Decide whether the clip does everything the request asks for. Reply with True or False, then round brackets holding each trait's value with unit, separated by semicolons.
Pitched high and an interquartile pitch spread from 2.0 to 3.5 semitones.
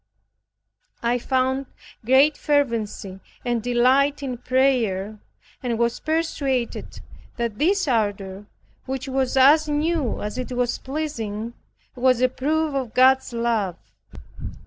True (255 Hz; 3.0 semitones)